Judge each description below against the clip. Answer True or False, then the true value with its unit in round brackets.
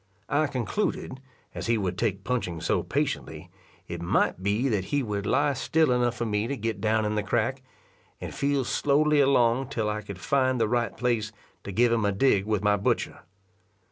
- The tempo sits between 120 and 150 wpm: False (195 wpm)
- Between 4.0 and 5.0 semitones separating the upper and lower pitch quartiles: True (4.4 semitones)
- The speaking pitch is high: False (115 Hz)